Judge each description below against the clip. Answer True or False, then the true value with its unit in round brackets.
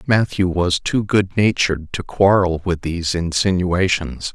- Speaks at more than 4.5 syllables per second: False (4.3 syllables/s)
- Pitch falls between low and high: False (90 Hz)